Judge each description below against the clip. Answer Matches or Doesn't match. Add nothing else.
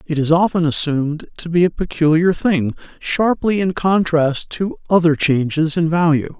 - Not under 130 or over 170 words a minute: Matches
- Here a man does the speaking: Matches